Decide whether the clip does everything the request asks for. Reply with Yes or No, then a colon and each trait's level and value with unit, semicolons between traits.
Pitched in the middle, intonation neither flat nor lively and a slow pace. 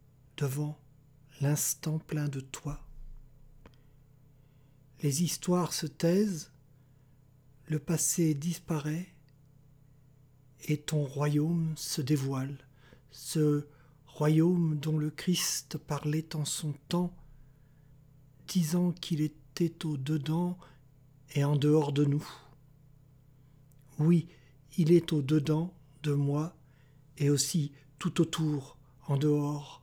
No: medium, 145 Hz; narrow, 2.2 semitones; slow, 95 wpm